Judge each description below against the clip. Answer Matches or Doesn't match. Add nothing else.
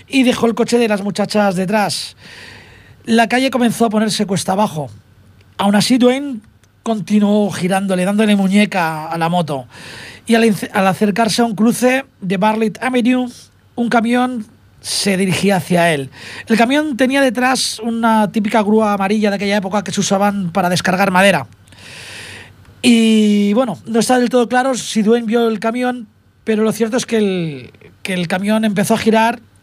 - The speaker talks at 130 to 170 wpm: Matches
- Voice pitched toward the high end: Matches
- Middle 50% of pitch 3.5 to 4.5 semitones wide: Matches